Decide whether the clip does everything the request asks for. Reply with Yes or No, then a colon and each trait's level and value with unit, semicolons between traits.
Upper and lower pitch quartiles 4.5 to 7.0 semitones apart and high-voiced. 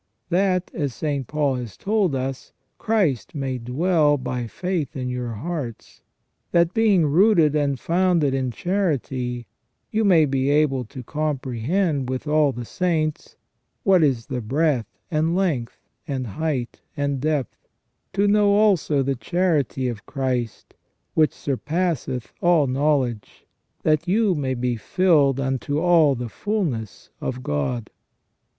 No: average, 5.2 semitones; medium, 145 Hz